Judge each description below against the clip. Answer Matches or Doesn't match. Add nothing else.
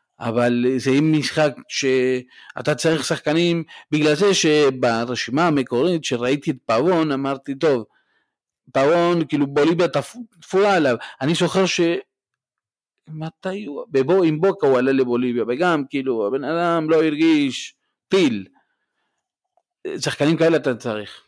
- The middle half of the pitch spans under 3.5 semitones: Doesn't match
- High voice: Doesn't match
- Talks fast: Doesn't match